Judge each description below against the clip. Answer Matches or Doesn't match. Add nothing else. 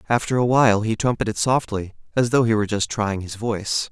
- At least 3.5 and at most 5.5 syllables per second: Doesn't match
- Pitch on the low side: Matches